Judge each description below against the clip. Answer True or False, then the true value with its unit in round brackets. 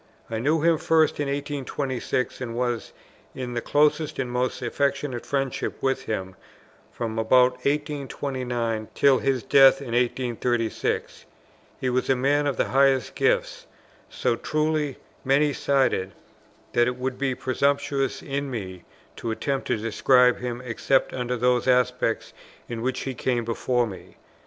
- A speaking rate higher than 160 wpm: False (145 wpm)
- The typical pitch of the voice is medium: False (130 Hz)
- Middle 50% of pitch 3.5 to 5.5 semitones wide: False (2.6 semitones)